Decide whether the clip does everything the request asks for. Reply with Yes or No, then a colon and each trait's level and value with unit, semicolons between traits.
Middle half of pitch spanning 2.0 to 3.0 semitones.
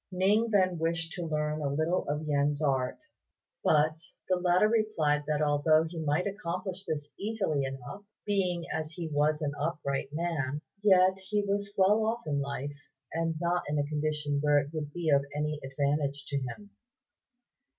No: average, 3.9 semitones